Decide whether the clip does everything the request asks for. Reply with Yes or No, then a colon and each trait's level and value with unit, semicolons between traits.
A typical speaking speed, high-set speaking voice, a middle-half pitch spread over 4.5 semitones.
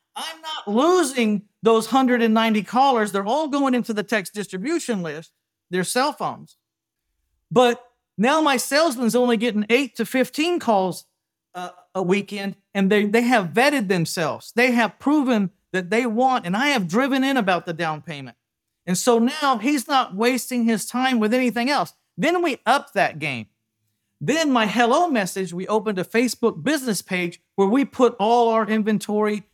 Yes: average, 170 wpm; high, 225 Hz; average, 5.1 semitones